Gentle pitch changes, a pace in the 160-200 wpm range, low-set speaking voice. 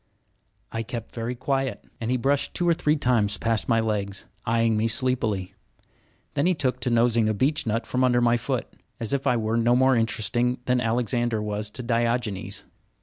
Yes: narrow, 2.2 semitones; average, 185 wpm; low, 115 Hz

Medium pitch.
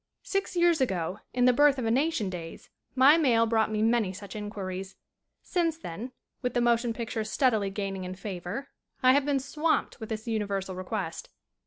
No: high, 225 Hz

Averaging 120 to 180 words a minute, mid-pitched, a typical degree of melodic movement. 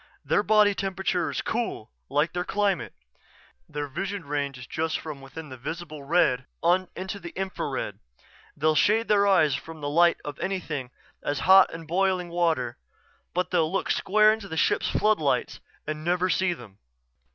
Yes: average, 165 wpm; medium, 170 Hz; average, 4.5 semitones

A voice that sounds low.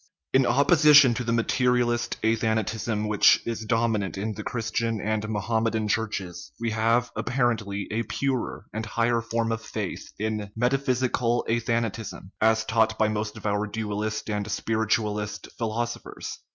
Yes: low, 110 Hz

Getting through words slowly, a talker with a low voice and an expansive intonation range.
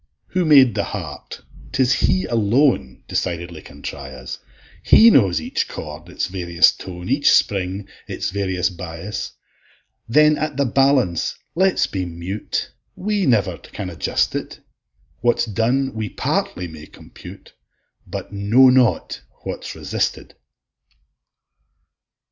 Yes: slow, 125 wpm; low, 100 Hz; wide, 7.0 semitones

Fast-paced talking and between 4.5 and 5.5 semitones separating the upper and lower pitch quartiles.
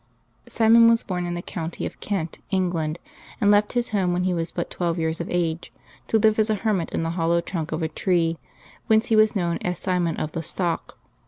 No: fast, 225 wpm; average, 3.8 semitones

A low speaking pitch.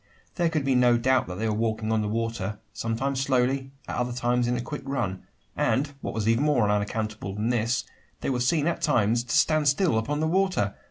Yes: low, 120 Hz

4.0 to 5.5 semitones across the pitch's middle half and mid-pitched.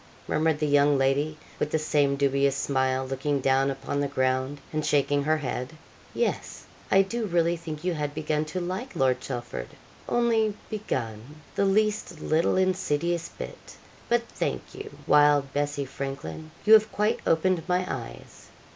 Yes: average, 4.7 semitones; medium, 150 Hz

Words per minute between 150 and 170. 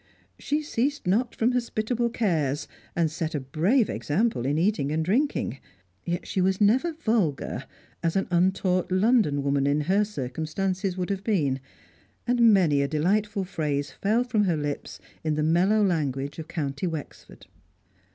Yes: average, 155 wpm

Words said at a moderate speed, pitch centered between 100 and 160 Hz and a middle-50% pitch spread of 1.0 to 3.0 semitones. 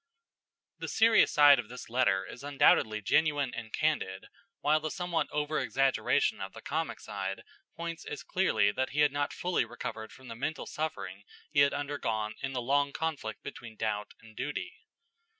No: average, 170 wpm; medium, 140 Hz; average, 5.3 semitones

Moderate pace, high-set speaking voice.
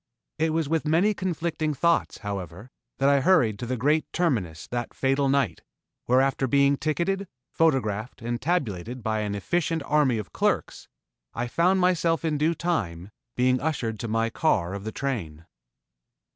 No: average, 160 wpm; low, 135 Hz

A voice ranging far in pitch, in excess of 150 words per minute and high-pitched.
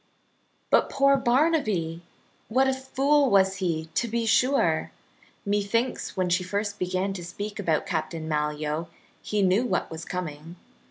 No: wide, 6.2 semitones; average, 145 wpm; high, 195 Hz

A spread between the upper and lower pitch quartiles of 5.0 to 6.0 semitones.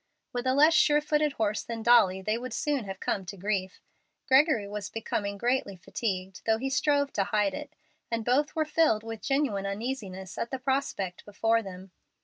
Yes: average, 5.3 semitones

